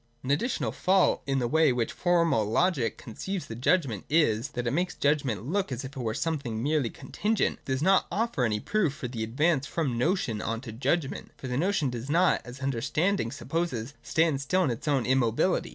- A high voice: No, low, 135 Hz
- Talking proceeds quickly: Yes, fast, 215 wpm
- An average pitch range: No, wide, 6.0 semitones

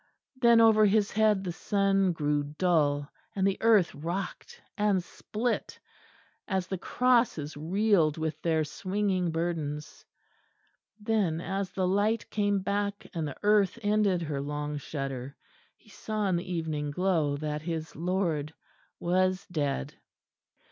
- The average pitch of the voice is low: No, medium, 180 Hz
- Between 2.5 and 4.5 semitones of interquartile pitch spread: No, average, 4.9 semitones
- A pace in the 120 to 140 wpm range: Yes, slow, 135 wpm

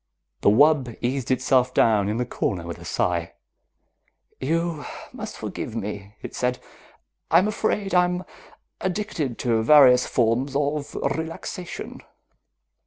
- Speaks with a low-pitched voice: Yes, low, 130 Hz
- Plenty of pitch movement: Yes, wide, 5.9 semitones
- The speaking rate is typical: No, slow, 120 wpm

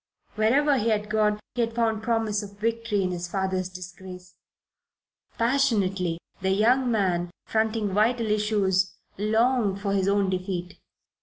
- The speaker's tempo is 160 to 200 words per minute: No, average, 140 wpm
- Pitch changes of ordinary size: Yes, average, 3.0 semitones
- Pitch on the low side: No, high, 210 Hz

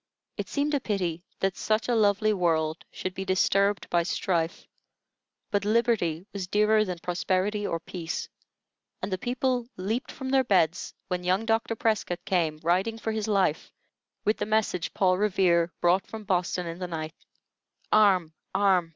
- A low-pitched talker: No, high, 190 Hz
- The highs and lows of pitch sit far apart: No, average, 3.5 semitones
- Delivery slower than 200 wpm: Yes, average, 160 wpm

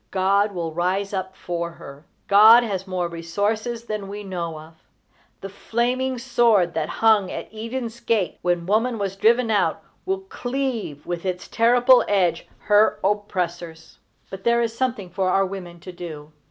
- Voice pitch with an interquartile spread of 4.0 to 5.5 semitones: Yes, average, 4.6 semitones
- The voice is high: Yes, high, 200 Hz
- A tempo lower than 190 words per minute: Yes, average, 160 wpm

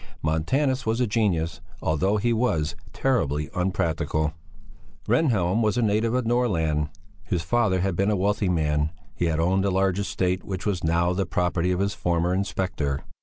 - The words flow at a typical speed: Yes, average, 170 wpm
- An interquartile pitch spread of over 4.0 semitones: Yes, average, 4.6 semitones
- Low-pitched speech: Yes, very low, 95 Hz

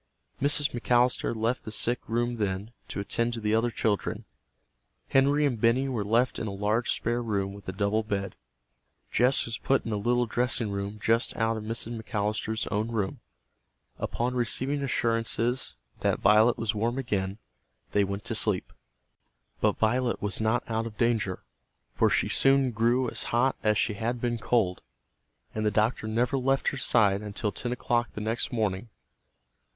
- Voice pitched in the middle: No, low, 115 Hz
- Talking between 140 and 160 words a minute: No, average, 170 wpm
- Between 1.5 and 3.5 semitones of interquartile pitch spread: Yes, narrow, 2.4 semitones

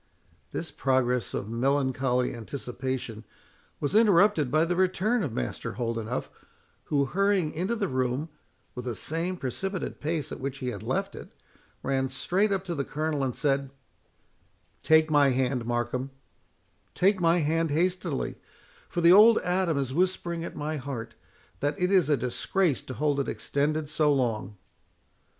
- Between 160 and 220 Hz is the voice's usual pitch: No, medium, 145 Hz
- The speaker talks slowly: No, average, 150 wpm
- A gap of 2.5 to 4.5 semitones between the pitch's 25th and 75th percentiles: No, average, 5.2 semitones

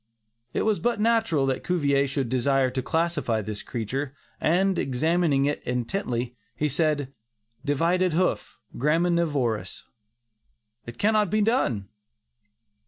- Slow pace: Yes, slow, 115 wpm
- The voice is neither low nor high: Yes, medium, 145 Hz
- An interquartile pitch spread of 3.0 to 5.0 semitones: No, wide, 5.6 semitones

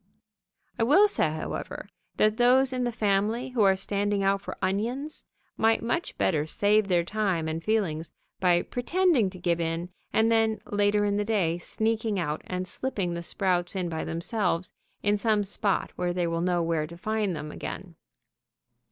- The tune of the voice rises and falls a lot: No, average, 4.1 semitones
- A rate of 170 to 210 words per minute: Yes, average, 175 wpm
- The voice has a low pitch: No, high, 200 Hz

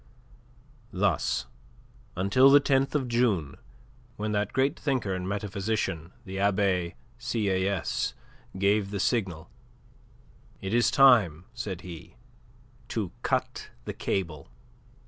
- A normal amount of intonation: Yes, average, 4.1 semitones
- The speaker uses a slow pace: Yes, slow, 105 wpm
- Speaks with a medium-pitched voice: No, low, 100 Hz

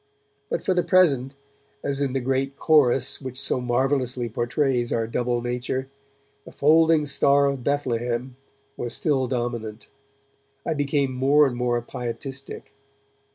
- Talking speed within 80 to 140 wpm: Yes, slow, 135 wpm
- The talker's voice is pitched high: No, low, 130 Hz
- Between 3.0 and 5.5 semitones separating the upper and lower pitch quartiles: No, narrow, 2.5 semitones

